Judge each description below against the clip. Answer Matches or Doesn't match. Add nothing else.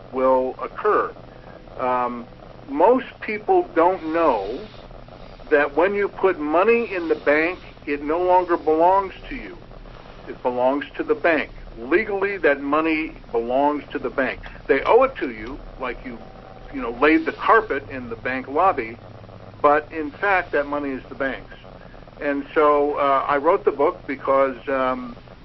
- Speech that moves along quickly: Doesn't match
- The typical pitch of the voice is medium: Matches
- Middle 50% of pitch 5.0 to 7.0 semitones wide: Matches